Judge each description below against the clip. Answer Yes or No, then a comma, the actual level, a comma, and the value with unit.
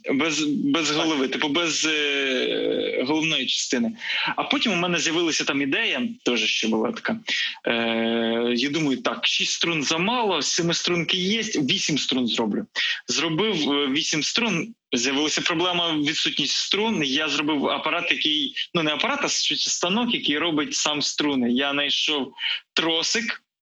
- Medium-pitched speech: Yes, medium, 165 Hz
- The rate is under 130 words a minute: No, average, 140 wpm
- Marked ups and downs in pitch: Yes, wide, 8.1 semitones